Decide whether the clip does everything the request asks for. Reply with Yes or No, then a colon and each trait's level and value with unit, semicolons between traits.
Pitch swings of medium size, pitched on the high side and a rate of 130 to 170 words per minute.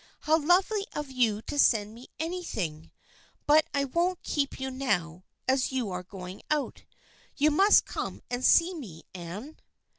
No: wide, 7.4 semitones; very high, 265 Hz; average, 155 wpm